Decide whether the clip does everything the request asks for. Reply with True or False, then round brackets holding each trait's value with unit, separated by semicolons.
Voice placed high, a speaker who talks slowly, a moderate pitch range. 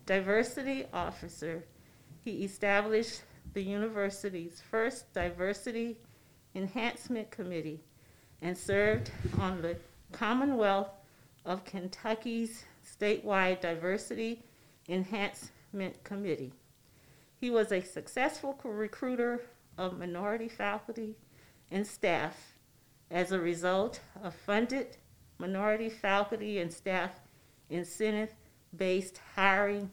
True (195 Hz; 85 wpm; 4.0 semitones)